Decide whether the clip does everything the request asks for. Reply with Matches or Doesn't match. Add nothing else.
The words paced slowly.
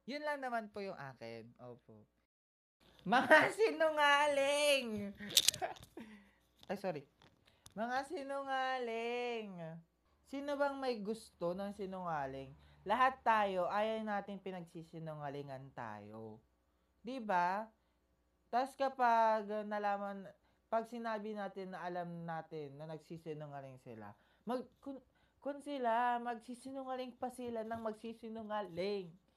Matches